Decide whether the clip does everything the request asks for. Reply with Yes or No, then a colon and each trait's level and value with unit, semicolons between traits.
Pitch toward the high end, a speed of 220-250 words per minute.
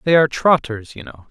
No: low, 135 Hz; fast, 230 wpm